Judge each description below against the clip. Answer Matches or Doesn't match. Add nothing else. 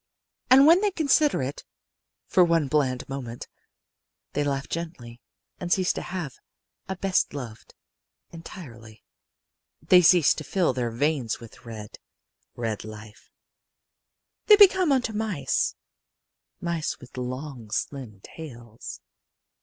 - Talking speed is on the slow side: Matches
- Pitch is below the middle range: Doesn't match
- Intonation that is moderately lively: Doesn't match